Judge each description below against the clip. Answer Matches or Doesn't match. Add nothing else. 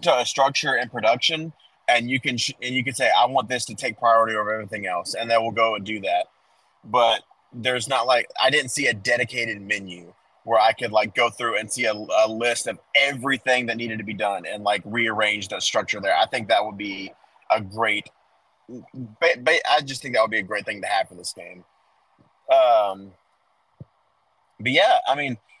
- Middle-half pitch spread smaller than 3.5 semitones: Matches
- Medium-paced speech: Doesn't match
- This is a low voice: Matches